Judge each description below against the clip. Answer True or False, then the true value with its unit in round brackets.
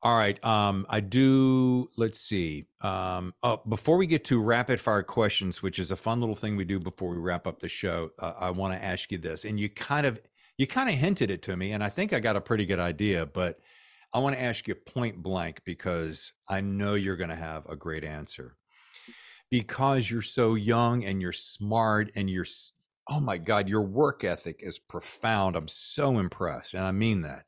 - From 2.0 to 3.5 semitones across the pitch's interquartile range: False (4.1 semitones)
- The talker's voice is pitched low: True (105 Hz)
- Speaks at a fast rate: True (215 wpm)